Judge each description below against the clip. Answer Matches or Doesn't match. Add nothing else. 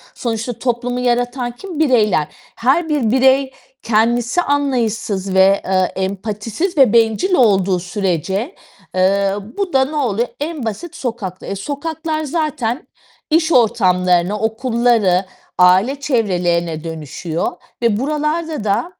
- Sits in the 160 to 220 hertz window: Doesn't match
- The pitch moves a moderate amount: Doesn't match